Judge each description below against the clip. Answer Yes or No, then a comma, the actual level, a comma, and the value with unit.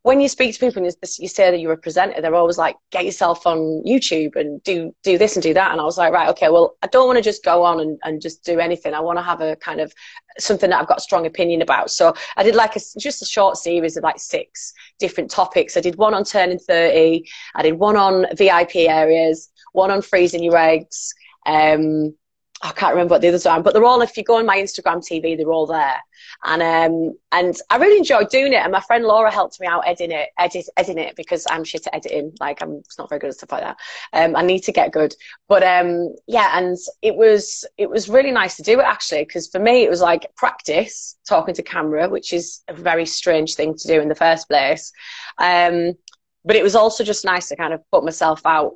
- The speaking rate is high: Yes, fast, 250 wpm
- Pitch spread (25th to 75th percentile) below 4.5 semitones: No, average, 4.8 semitones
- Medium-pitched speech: Yes, medium, 175 Hz